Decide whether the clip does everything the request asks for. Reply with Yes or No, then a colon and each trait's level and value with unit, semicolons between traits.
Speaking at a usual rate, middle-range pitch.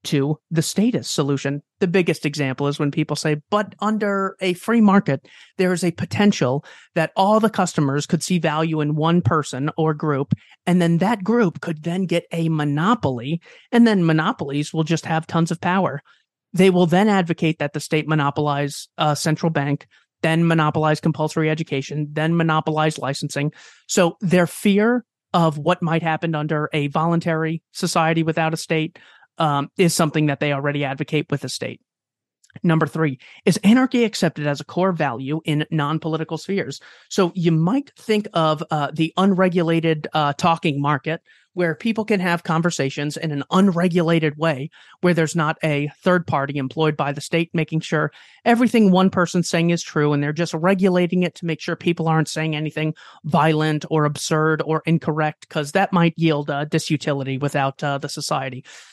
Yes: average, 175 wpm; medium, 160 Hz